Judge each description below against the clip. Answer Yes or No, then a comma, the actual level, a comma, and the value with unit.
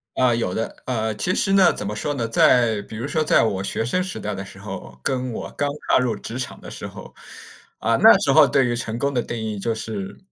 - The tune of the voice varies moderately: Yes, average, 3.2 semitones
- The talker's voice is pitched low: Yes, low, 115 Hz